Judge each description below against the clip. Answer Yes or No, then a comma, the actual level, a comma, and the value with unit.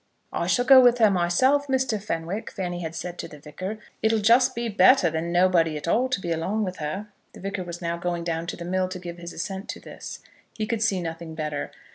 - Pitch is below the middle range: No, medium, 185 Hz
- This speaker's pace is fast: Yes, fast, 235 wpm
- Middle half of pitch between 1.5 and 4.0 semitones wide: No, average, 4.4 semitones